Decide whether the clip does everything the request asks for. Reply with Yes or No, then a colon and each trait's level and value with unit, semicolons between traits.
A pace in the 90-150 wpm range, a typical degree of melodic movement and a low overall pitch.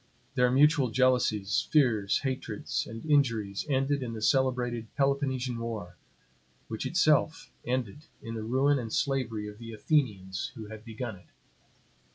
Yes: average, 140 wpm; average, 3.8 semitones; low, 125 Hz